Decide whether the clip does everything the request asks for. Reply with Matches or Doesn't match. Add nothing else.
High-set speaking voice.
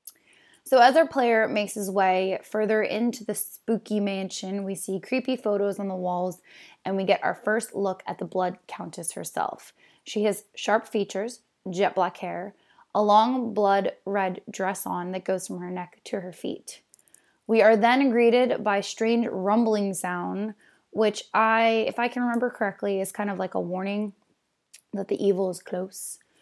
Matches